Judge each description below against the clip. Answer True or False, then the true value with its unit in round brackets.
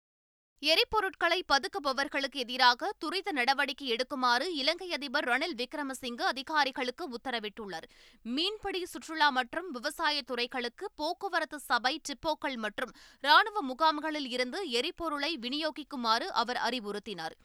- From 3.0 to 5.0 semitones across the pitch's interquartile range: True (4.5 semitones)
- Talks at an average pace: True (95 wpm)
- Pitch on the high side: True (285 Hz)